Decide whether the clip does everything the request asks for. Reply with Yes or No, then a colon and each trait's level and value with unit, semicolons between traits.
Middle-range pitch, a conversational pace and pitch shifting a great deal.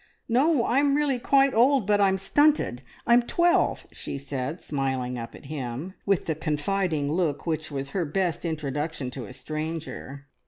Yes: medium, 160 Hz; average, 160 wpm; wide, 8.3 semitones